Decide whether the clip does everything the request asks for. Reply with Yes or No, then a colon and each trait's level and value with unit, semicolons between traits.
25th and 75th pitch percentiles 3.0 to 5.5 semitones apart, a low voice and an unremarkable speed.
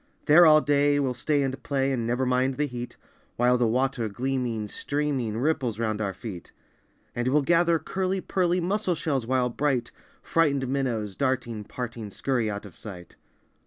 Yes: average, 3.9 semitones; low, 130 Hz; average, 165 wpm